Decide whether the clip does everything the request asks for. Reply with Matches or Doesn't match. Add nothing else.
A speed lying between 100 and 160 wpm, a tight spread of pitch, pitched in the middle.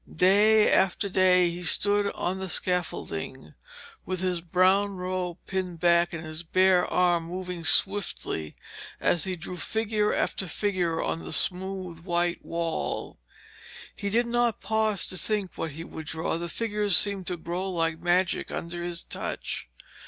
Matches